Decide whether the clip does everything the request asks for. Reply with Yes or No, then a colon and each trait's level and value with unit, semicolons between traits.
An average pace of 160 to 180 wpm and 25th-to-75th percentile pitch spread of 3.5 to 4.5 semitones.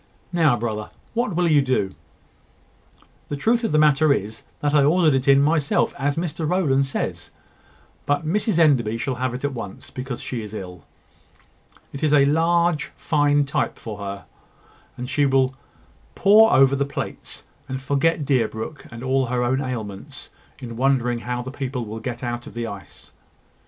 Yes: average, 170 wpm; average, 3.9 semitones